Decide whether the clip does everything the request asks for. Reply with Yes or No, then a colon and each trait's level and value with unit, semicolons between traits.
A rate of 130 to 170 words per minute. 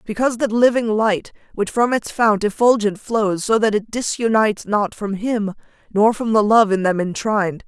No: average, 190 wpm